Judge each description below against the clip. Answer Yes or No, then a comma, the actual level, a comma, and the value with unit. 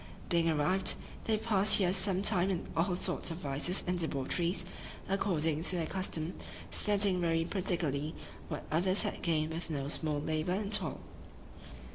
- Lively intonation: No, average, 3.3 semitones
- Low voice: No, medium, 175 Hz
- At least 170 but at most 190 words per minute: No, average, 155 wpm